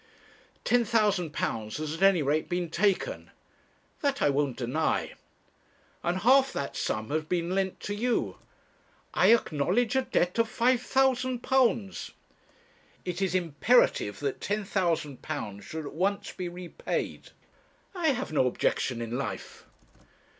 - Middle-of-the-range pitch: Yes, medium, 180 Hz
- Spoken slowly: Yes, slow, 130 wpm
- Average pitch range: No, wide, 7.7 semitones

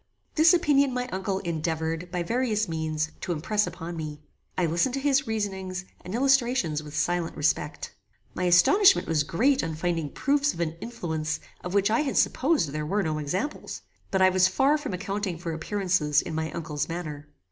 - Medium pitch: Yes, medium, 180 Hz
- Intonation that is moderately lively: No, wide, 6.5 semitones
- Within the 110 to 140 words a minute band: No, average, 180 wpm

